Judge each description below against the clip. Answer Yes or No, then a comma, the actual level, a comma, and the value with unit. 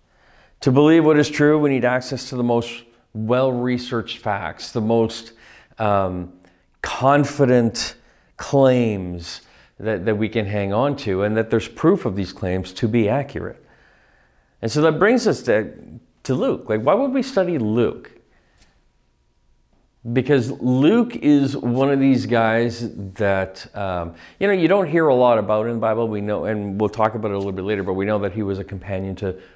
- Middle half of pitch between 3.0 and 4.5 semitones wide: No, average, 5.0 semitones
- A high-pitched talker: No, low, 115 Hz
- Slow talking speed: No, average, 180 wpm